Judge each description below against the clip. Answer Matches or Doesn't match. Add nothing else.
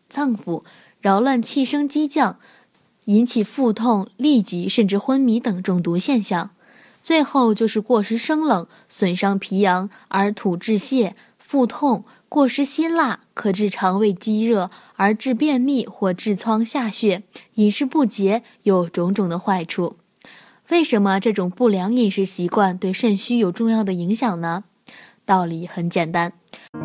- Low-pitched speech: Doesn't match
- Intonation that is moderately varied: Matches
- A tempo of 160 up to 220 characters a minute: Matches